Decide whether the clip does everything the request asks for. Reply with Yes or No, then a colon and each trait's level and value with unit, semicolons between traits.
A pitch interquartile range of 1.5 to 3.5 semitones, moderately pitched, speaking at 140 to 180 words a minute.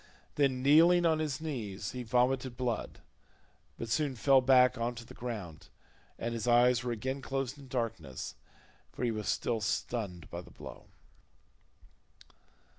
No: average, 2.9 semitones; low, 125 Hz; average, 150 wpm